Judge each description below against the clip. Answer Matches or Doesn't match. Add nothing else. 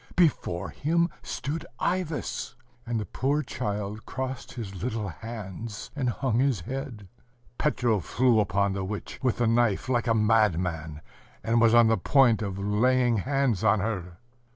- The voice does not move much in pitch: Doesn't match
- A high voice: Doesn't match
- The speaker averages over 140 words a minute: Matches